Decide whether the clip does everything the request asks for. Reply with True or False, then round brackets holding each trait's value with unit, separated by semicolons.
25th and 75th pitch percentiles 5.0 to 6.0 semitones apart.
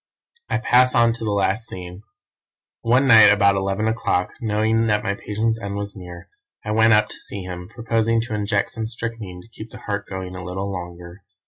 False (2.8 semitones)